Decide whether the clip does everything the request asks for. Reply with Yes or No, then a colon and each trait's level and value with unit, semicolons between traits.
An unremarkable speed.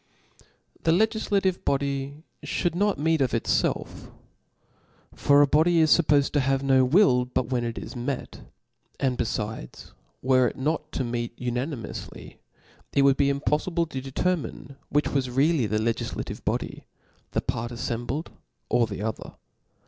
Yes: average, 155 wpm